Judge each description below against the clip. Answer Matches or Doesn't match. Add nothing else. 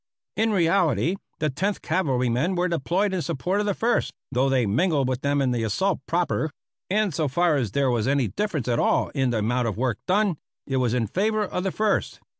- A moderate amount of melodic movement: Doesn't match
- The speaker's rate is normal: Doesn't match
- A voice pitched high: Doesn't match